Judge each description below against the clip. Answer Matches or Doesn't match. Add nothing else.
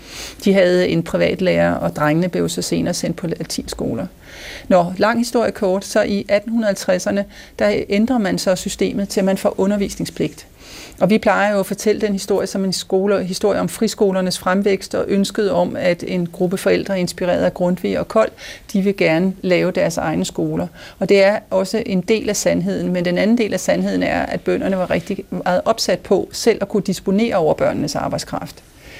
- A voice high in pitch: Matches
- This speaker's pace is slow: Doesn't match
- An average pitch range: Doesn't match